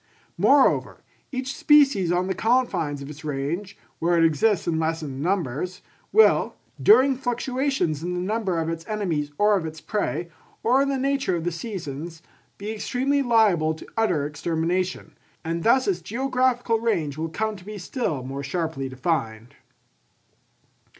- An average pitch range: No, wide, 6.4 semitones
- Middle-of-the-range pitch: Yes, medium, 180 Hz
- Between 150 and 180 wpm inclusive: Yes, average, 155 wpm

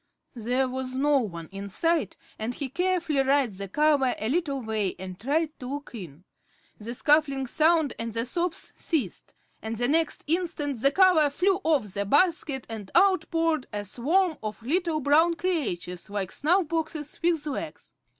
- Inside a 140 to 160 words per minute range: No, average, 170 wpm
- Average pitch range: No, wide, 6.2 semitones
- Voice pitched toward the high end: Yes, very high, 280 Hz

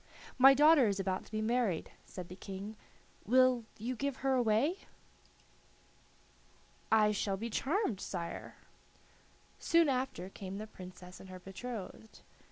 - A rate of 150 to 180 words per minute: No, slow, 135 wpm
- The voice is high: Yes, high, 220 Hz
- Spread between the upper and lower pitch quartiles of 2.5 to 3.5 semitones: No, average, 5.0 semitones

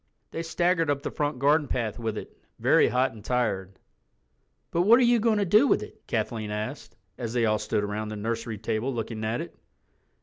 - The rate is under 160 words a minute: No, fast, 205 wpm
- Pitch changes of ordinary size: No, wide, 6.2 semitones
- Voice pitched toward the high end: No, low, 120 Hz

